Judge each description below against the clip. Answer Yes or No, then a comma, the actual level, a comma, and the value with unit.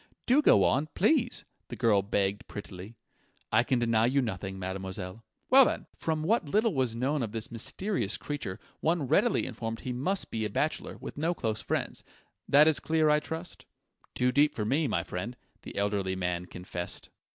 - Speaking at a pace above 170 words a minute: Yes, average, 180 wpm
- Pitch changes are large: Yes, wide, 7.3 semitones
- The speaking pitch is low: Yes, low, 120 Hz